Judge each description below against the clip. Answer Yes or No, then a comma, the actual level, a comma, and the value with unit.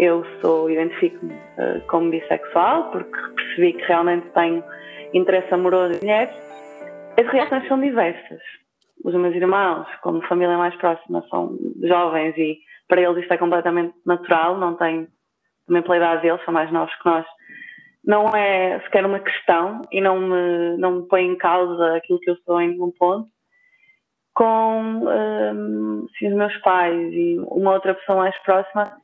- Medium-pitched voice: Yes, medium, 175 Hz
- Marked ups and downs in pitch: No, average, 2.7 semitones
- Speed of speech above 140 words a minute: Yes, average, 160 wpm